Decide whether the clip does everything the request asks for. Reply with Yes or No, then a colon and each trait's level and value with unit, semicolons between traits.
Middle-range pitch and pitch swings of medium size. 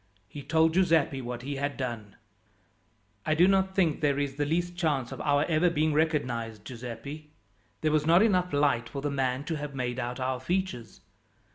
Yes: medium, 145 Hz; average, 4.1 semitones